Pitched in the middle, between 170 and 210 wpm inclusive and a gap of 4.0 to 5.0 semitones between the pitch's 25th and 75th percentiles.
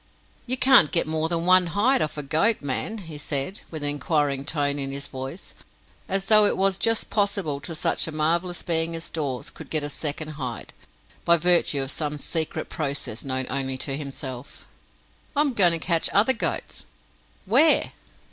Yes: medium, 160 Hz; average, 185 wpm; average, 4.7 semitones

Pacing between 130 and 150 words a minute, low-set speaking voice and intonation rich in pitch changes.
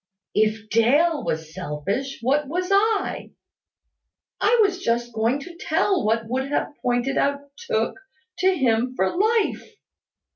No: slow, 135 wpm; very high, 275 Hz; wide, 8.1 semitones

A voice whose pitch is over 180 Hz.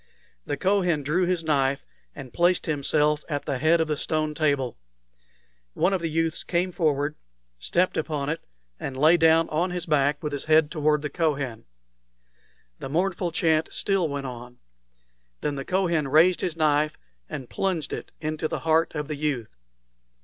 No: medium, 155 Hz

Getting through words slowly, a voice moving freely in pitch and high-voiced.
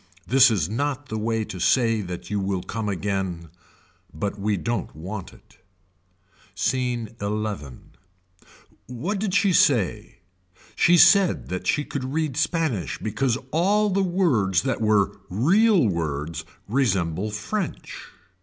No: slow, 130 wpm; wide, 7.5 semitones; low, 110 Hz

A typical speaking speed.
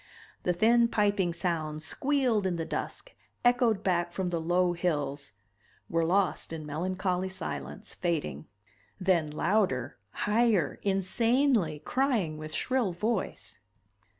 No: slow, 120 wpm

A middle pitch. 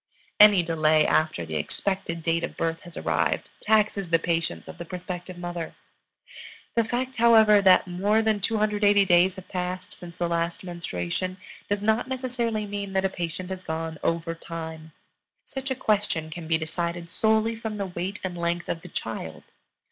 Yes: medium, 180 Hz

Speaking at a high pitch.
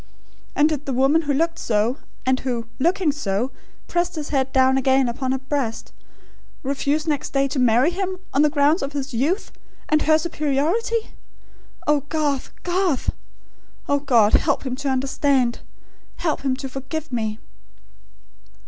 Yes: very high, 280 Hz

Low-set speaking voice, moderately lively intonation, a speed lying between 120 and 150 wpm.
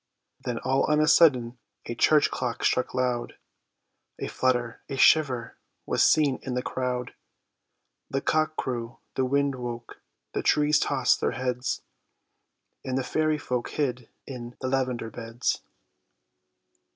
No: low, 130 Hz; narrow, 2.3 semitones; average, 140 wpm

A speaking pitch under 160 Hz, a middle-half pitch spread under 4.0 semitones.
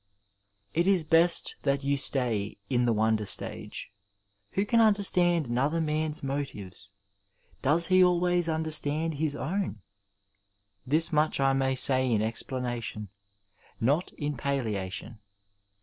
No: medium, 140 Hz; average, 5.3 semitones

